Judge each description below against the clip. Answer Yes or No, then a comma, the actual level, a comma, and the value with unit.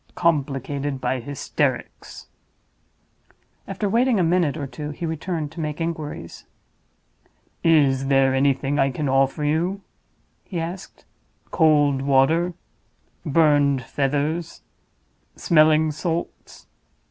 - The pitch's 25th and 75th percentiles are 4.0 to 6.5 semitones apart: No, average, 3.3 semitones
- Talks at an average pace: No, slow, 100 wpm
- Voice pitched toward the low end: No, medium, 150 Hz